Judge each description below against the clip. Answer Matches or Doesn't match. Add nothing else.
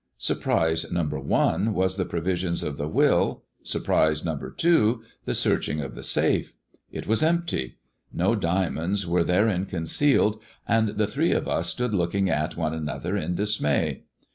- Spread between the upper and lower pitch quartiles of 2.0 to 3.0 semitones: Doesn't match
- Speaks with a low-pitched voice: Matches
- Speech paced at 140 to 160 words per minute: Matches